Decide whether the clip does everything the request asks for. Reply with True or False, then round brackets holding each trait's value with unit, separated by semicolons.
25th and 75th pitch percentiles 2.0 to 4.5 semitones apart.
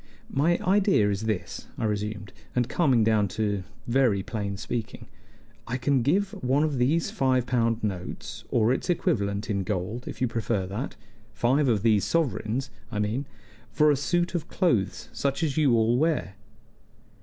False (5.1 semitones)